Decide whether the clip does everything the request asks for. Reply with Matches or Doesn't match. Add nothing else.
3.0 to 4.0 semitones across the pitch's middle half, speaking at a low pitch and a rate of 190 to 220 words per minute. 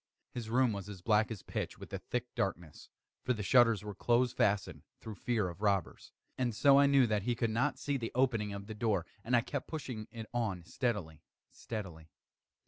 Matches